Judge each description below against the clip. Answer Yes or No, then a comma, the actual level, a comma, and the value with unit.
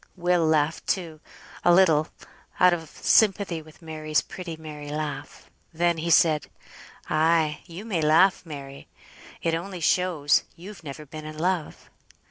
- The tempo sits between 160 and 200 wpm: No, average, 140 wpm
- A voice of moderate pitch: Yes, medium, 160 Hz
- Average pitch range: No, narrow, 2.3 semitones